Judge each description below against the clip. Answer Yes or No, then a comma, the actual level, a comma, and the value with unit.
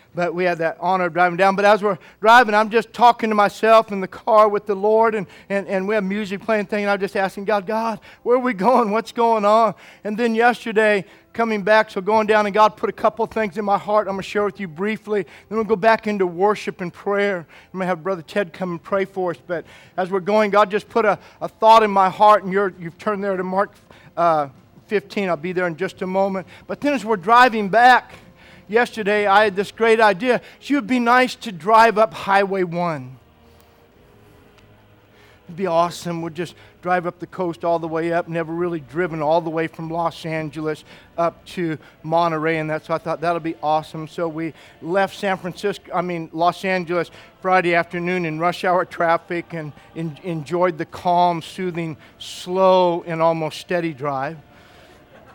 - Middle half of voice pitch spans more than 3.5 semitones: Yes, average, 4.1 semitones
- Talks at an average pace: No, fast, 210 wpm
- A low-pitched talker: No, medium, 185 Hz